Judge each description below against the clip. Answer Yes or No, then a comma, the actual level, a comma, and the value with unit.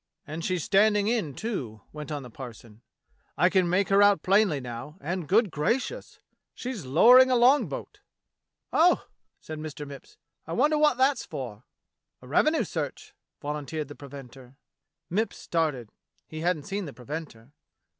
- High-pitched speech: No, medium, 160 Hz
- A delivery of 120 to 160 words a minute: Yes, average, 155 wpm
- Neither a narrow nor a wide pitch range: No, wide, 7.4 semitones